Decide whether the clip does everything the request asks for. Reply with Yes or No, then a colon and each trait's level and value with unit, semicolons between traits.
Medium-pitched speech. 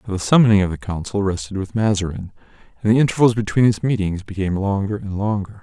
No: low, 100 Hz